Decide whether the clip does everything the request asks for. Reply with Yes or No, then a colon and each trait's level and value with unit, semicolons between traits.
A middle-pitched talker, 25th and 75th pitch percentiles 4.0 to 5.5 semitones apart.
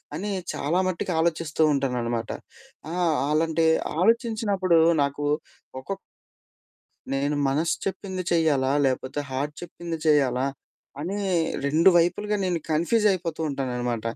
Yes: medium, 160 Hz; average, 4.7 semitones